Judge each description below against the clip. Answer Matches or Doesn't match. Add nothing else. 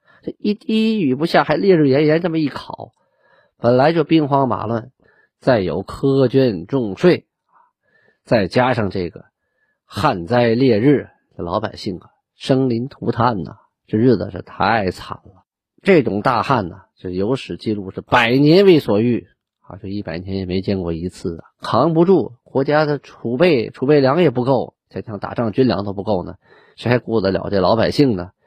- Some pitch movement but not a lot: Doesn't match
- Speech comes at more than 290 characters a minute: Doesn't match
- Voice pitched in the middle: Doesn't match